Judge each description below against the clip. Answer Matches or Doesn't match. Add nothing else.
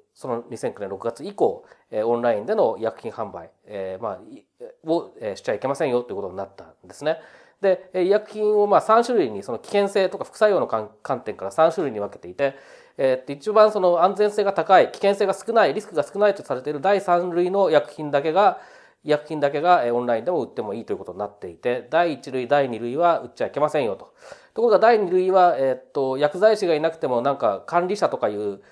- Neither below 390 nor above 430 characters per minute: Matches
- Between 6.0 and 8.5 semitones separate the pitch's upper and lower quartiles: Matches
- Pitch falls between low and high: Matches